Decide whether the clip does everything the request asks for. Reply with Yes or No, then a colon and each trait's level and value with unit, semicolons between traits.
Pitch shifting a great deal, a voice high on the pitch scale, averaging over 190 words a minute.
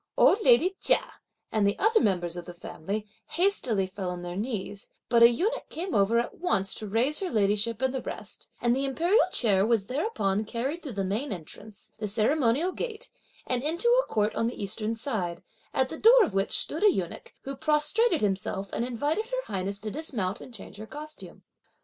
Yes: wide, 7.5 semitones; high, 235 Hz; average, 200 wpm